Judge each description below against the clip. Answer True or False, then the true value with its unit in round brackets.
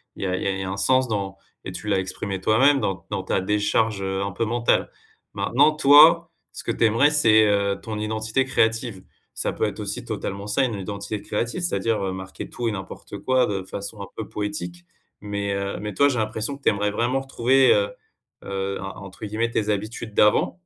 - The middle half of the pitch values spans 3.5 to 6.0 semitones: False (3.1 semitones)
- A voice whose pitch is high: False (105 Hz)